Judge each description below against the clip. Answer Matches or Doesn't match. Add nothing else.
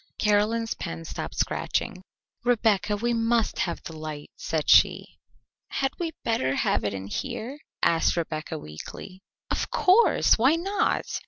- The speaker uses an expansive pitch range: Matches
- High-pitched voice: Matches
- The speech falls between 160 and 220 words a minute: Doesn't match